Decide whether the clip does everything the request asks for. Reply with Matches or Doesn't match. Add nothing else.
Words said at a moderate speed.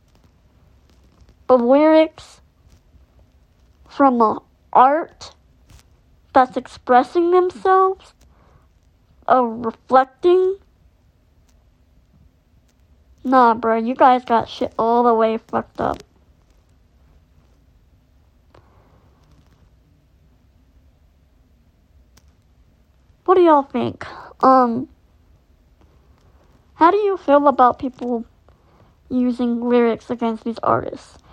Doesn't match